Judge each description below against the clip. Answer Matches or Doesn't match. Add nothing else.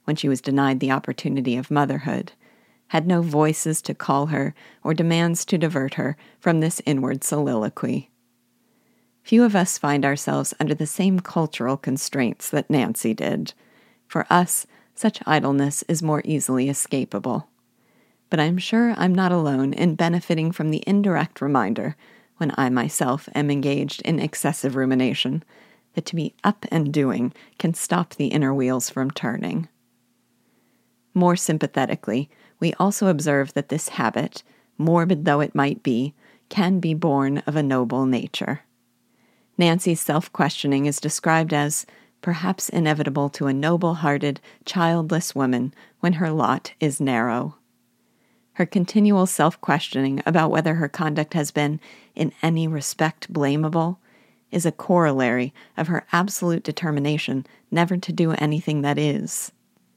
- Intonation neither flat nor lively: Matches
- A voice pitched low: Doesn't match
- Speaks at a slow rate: Doesn't match